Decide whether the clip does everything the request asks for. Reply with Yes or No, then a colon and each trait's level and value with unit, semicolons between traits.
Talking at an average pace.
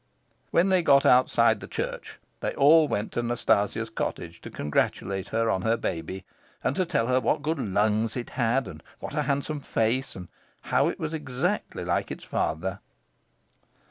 Yes: average, 175 wpm